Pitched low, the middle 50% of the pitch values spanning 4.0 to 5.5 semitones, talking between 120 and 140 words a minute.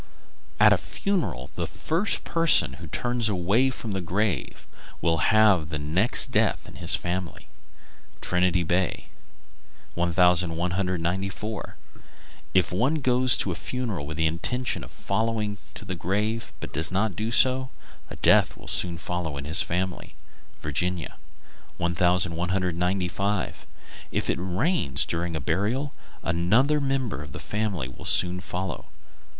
Yes: very low, 95 Hz; average, 4.4 semitones; slow, 135 wpm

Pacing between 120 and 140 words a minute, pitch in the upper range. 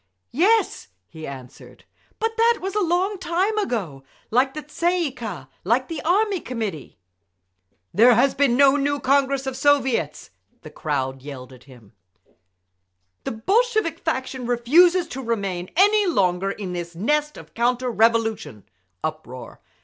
Yes: slow, 135 wpm; very high, 255 Hz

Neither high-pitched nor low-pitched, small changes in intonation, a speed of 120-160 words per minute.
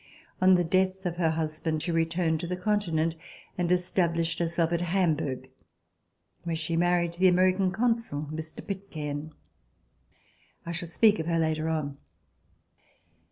Yes: medium, 170 Hz; narrow, 2.3 semitones; average, 140 wpm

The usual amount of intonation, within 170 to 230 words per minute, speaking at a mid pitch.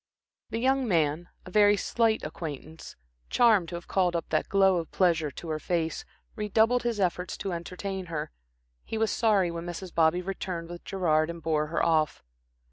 Yes: average, 3.7 semitones; average, 180 wpm; medium, 175 Hz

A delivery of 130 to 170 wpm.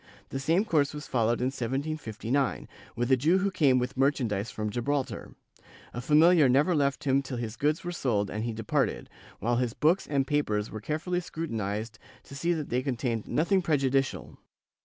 No: average, 180 wpm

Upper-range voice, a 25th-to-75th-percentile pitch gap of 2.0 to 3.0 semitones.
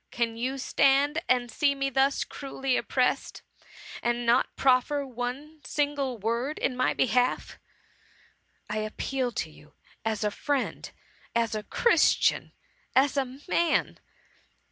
Yes: very high, 255 Hz; average, 2.7 semitones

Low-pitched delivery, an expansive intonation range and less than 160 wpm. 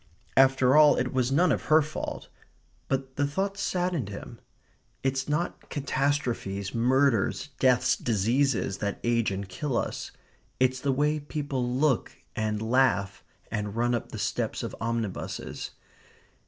No: low, 130 Hz; average, 4.0 semitones; average, 140 wpm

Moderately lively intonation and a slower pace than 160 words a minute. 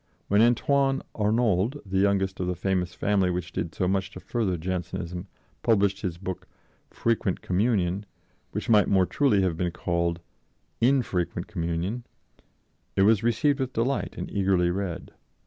Yes: average, 3.9 semitones; average, 145 wpm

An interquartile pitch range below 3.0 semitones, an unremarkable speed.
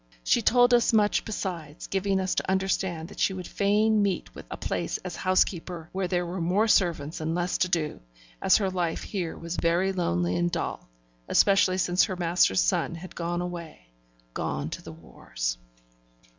Yes: narrow, 2.6 semitones; average, 180 wpm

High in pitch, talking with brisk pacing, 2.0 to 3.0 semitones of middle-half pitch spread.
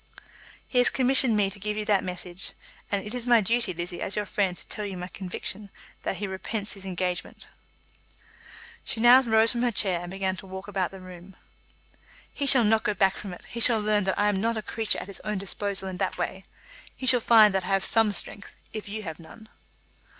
Yes: high, 205 Hz; fast, 225 wpm; average, 2.7 semitones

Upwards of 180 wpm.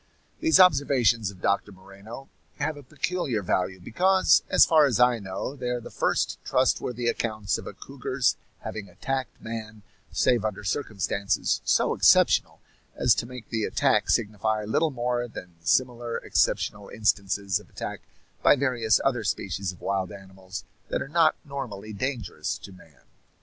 No: average, 155 wpm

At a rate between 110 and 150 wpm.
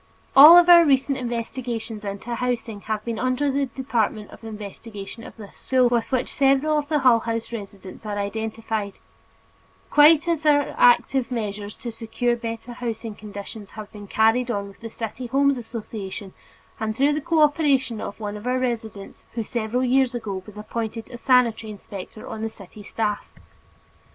No: average, 170 wpm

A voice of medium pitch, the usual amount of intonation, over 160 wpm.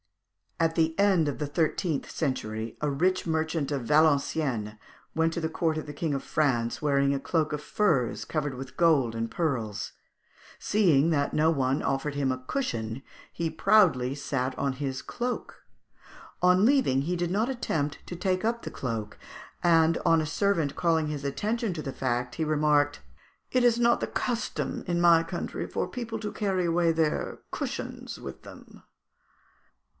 Yes: medium, 155 Hz; average, 4.2 semitones; average, 170 wpm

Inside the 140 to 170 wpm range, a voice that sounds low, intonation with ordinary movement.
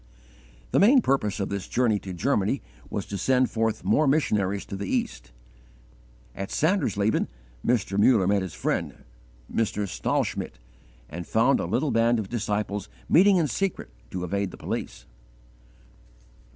Yes: average, 145 wpm; low, 105 Hz; average, 4.7 semitones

